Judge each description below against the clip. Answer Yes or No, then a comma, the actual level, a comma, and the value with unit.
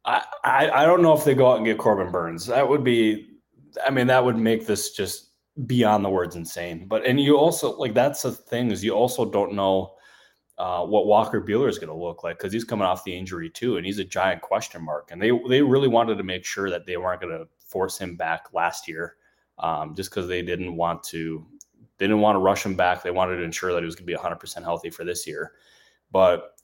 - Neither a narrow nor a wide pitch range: No, wide, 5.7 semitones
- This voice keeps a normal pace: No, fast, 245 wpm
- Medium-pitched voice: No, low, 100 Hz